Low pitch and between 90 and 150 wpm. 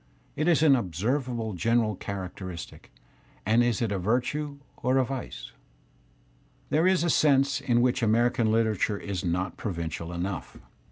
Yes: low, 115 Hz; average, 145 wpm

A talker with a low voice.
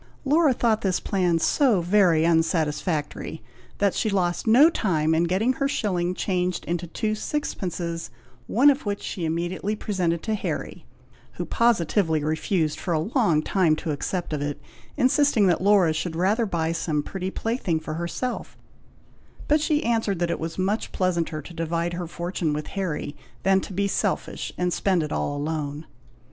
No: medium, 180 Hz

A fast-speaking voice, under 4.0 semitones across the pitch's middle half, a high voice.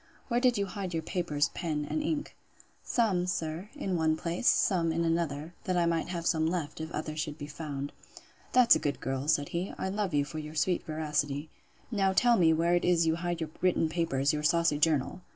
No: fast, 210 wpm; average, 2.9 semitones; medium, 165 Hz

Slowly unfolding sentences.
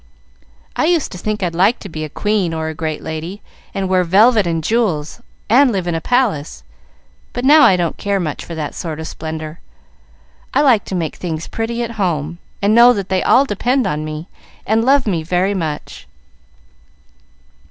No: average, 190 wpm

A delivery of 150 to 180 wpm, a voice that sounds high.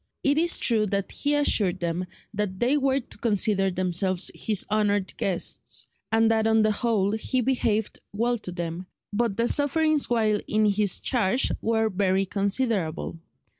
Yes: average, 160 wpm; high, 215 Hz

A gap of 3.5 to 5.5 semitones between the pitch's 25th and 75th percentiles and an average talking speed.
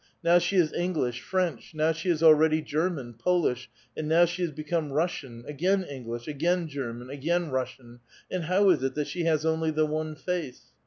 Yes: average, 3.9 semitones; average, 190 wpm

